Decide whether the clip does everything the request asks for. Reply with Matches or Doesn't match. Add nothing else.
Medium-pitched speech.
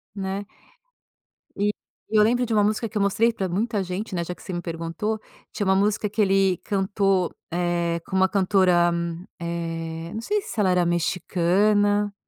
Doesn't match